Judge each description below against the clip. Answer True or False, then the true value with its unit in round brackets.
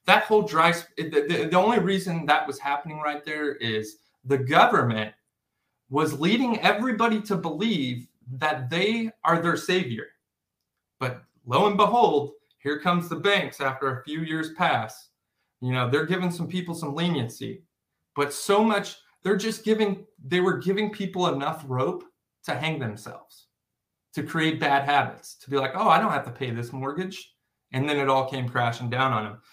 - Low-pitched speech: False (155 Hz)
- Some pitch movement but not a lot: False (5.8 semitones)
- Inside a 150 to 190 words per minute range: True (175 wpm)